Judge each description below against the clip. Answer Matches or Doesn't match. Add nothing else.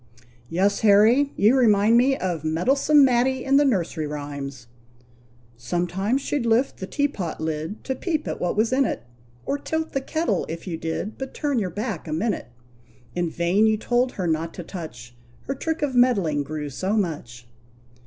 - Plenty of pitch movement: Matches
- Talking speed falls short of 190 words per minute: Matches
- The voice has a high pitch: Matches